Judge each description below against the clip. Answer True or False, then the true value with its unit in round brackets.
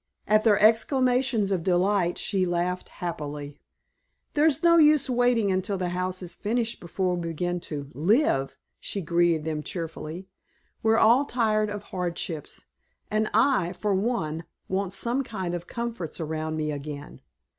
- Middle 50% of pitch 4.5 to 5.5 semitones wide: True (5.0 semitones)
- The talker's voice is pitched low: False (185 Hz)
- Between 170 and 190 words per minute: False (145 wpm)